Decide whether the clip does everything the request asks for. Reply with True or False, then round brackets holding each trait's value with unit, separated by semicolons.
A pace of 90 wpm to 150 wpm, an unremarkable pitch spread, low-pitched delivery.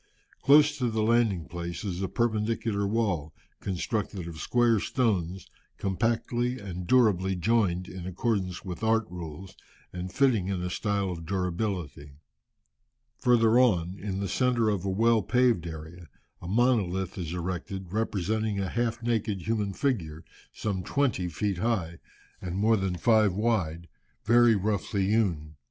True (140 wpm; 4.2 semitones; 100 Hz)